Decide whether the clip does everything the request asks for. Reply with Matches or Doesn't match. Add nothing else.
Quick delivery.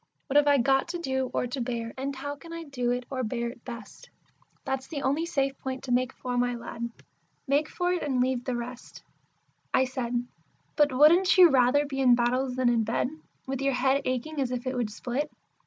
Matches